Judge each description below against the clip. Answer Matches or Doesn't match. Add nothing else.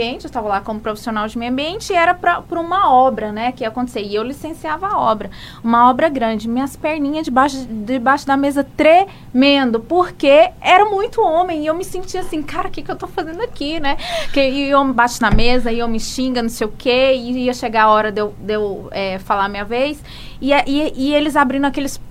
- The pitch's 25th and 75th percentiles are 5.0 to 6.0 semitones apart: Matches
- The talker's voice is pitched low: Doesn't match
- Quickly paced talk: Matches